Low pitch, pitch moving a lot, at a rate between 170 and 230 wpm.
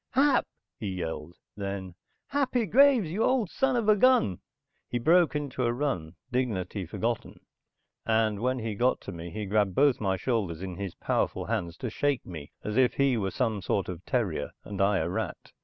Yes: low, 110 Hz; wide, 7.2 semitones; average, 190 wpm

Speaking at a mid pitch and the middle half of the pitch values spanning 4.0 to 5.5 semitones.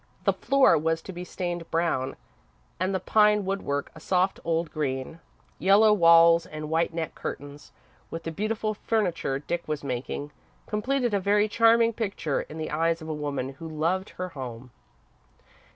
Yes: medium, 165 Hz; average, 4.7 semitones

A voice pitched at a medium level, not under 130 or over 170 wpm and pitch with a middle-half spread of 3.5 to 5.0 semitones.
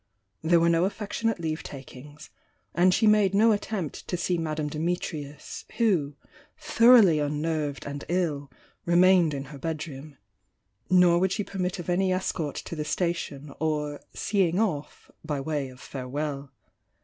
Yes: medium, 165 Hz; average, 155 wpm; average, 4.1 semitones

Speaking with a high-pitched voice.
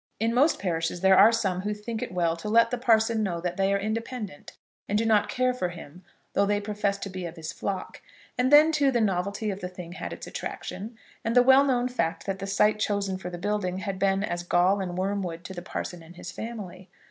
Yes: high, 200 Hz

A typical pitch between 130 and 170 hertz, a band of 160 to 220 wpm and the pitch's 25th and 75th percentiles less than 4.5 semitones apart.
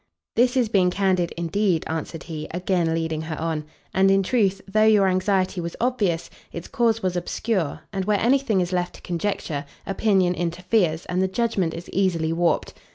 No: medium, 185 Hz; average, 180 wpm; average, 3.4 semitones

